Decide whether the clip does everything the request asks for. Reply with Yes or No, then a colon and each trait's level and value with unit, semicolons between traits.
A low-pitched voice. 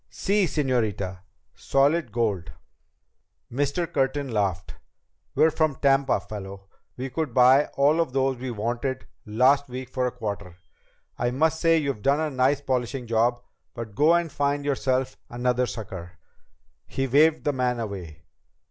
Yes: low, 130 Hz